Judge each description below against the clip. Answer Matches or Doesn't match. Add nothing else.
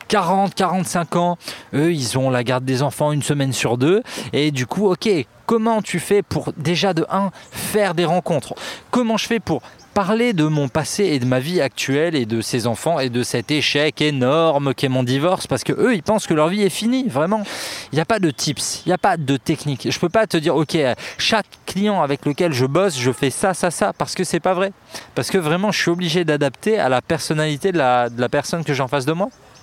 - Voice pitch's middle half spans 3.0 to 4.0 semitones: Doesn't match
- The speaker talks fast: Matches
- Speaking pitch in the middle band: Matches